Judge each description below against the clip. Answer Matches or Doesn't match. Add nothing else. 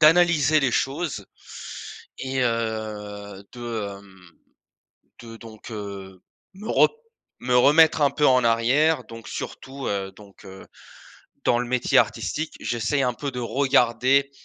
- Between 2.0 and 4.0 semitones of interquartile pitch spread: Doesn't match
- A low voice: Matches